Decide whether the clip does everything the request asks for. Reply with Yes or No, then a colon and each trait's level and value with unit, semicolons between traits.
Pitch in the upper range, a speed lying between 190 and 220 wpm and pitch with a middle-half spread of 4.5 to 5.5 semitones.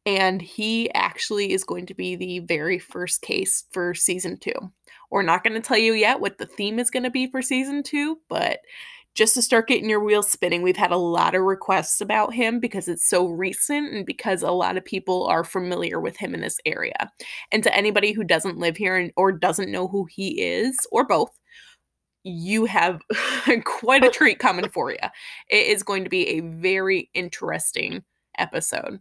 Yes: high, 200 Hz; average, 200 wpm; average, 5.2 semitones